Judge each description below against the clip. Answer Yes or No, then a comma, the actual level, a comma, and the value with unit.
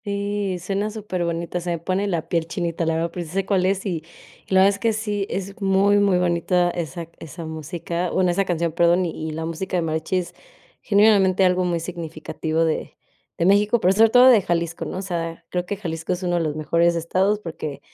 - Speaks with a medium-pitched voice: Yes, medium, 180 Hz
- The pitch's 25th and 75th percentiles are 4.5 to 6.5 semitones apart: No, average, 2.8 semitones